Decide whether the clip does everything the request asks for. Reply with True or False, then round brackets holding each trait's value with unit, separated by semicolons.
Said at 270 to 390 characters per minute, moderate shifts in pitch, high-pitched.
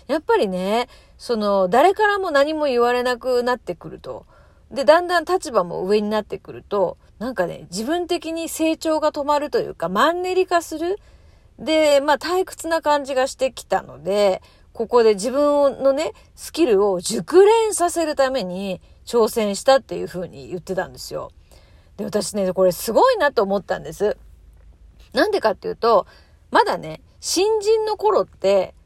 False (315 characters per minute; 8.8 semitones; 270 Hz)